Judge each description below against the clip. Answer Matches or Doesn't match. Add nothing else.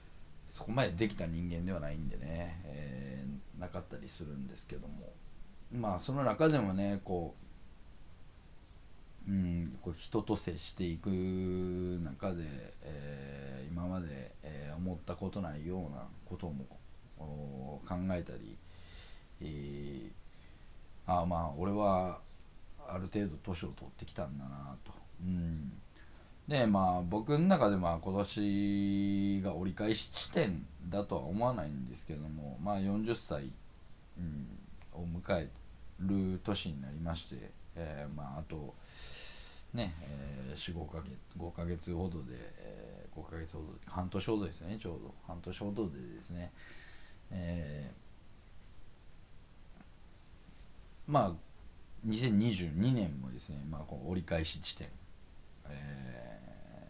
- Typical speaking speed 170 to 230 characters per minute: Matches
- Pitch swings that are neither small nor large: Matches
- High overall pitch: Doesn't match